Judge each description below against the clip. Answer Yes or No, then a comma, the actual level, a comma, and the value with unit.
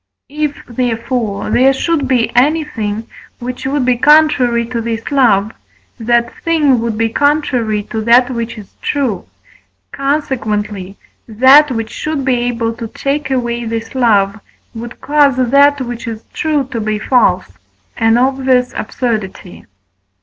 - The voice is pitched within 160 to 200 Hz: No, high, 245 Hz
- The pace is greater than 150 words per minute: No, slow, 135 wpm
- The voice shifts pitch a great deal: No, average, 3.2 semitones